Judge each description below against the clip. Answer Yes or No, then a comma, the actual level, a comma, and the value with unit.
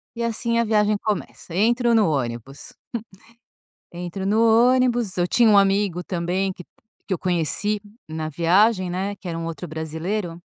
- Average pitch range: Yes, average, 4.3 semitones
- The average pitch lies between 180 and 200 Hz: Yes, high, 190 Hz